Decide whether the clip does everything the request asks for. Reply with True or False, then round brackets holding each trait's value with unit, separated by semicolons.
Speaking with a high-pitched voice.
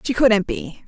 True (225 Hz)